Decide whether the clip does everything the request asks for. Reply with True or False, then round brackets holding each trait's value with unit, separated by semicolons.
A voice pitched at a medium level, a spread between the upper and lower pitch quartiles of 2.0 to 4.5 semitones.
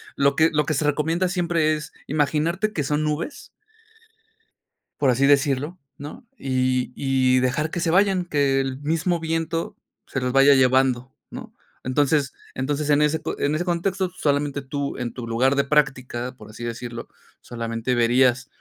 True (145 Hz; 3.4 semitones)